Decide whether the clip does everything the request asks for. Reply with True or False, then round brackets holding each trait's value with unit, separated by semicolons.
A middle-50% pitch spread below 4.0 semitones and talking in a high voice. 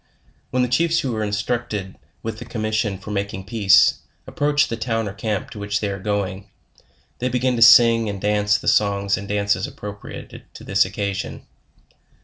False (2.4 semitones; 105 Hz)